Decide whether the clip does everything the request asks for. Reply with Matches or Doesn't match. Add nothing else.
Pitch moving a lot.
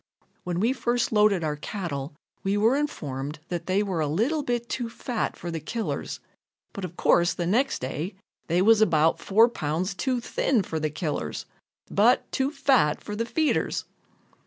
Matches